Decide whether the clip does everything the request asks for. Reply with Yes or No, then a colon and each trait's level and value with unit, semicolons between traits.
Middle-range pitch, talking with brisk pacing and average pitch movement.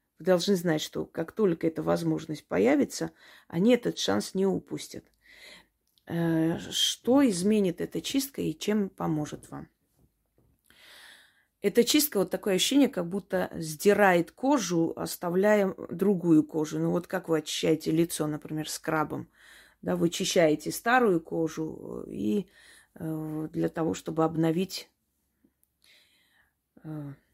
No: medium, 170 Hz; average, 115 wpm; average, 4.1 semitones